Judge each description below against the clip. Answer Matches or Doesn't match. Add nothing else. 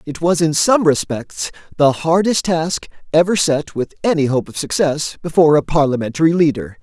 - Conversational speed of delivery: Matches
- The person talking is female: Doesn't match